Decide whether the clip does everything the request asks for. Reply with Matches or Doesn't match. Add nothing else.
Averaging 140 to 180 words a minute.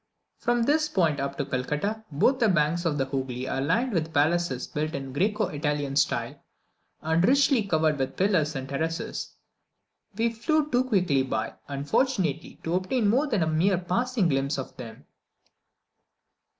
Matches